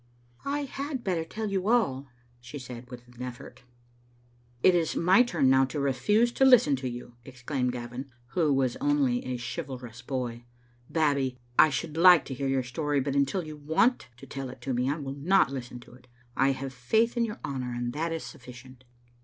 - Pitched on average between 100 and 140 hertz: Yes, low, 135 Hz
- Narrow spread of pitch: No, average, 5.2 semitones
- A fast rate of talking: Yes, fast, 210 wpm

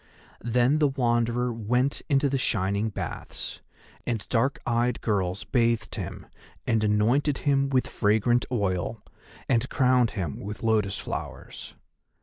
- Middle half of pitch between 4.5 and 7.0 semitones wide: No, average, 3.3 semitones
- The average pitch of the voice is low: Yes, low, 120 Hz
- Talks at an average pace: No, slow, 130 wpm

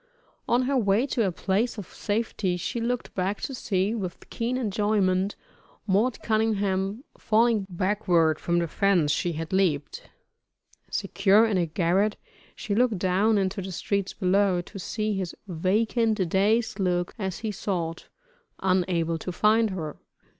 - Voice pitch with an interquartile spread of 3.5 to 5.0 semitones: No, average, 3.1 semitones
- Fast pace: No, average, 145 wpm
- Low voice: No, high, 195 Hz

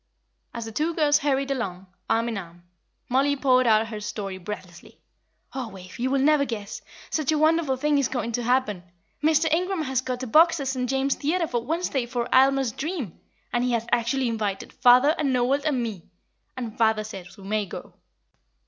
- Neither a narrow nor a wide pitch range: Yes, average, 4.2 semitones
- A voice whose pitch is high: Yes, very high, 255 Hz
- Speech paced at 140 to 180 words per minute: No, average, 195 wpm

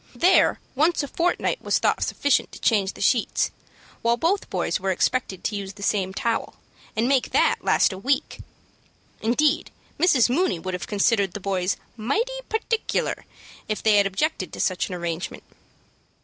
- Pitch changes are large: Yes, wide, 6.9 semitones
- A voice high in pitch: Yes, high, 225 Hz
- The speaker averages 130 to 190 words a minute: Yes, average, 165 wpm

